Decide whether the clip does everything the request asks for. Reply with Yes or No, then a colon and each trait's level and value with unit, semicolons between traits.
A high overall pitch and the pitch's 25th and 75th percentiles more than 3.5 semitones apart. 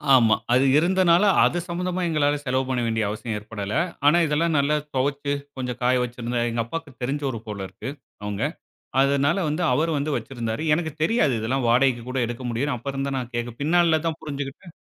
No: low, 135 Hz; average, 4.2 semitones